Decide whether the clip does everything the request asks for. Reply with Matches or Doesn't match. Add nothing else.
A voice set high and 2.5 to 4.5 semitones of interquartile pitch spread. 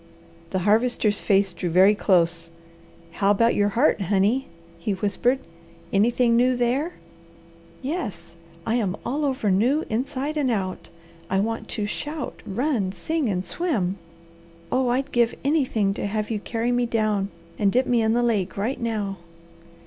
Matches